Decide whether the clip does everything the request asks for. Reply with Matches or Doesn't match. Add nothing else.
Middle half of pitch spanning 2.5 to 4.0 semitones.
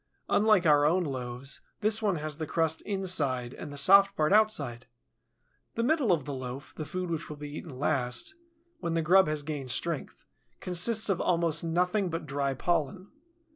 Doesn't match